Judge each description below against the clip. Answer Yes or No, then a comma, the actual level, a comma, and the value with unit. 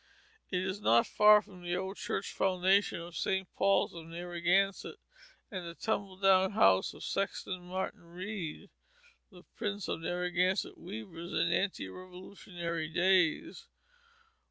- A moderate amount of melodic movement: No, narrow, 2.1 semitones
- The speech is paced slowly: Yes, slow, 130 wpm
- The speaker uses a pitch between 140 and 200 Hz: Yes, medium, 185 Hz